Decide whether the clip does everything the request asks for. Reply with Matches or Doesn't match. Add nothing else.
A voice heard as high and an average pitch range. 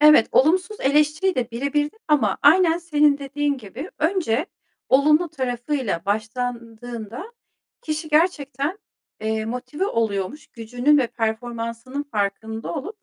Matches